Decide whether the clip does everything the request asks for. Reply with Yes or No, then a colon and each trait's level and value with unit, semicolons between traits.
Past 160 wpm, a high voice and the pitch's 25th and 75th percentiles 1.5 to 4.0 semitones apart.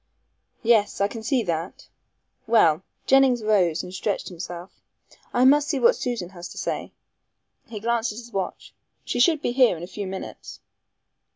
No: average, 170 wpm; high, 215 Hz; average, 4.9 semitones